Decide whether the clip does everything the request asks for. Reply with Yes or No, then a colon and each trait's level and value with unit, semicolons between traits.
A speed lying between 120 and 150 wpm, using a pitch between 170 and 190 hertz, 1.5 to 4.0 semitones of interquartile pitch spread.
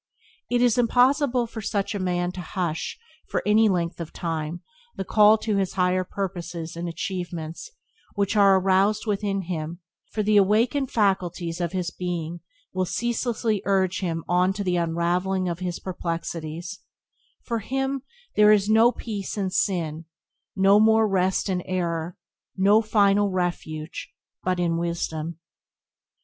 Yes: average, 145 wpm; medium, 185 Hz; average, 3.4 semitones